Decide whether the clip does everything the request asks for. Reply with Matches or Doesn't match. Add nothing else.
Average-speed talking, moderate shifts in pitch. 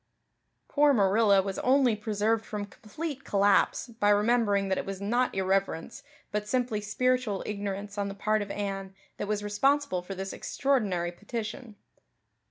Matches